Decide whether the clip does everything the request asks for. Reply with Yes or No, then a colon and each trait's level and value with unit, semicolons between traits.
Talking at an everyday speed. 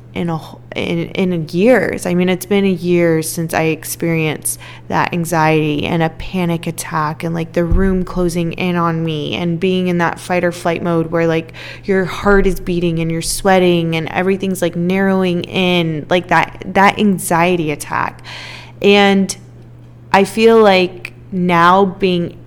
Yes: average, 165 wpm